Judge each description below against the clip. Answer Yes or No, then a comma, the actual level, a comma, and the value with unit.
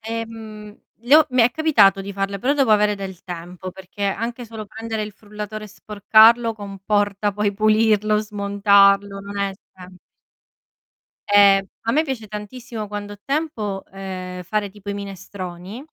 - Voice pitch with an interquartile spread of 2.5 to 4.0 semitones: No, narrow, 2.0 semitones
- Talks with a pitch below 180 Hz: No, high, 205 Hz